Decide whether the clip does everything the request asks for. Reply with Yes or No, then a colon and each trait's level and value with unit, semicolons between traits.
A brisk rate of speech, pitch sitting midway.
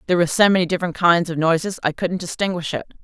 Yes: fast, 235 wpm; medium, 170 Hz